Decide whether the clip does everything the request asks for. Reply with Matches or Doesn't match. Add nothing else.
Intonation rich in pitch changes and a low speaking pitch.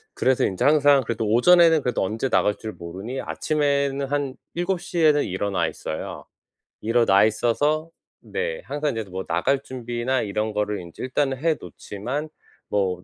Matches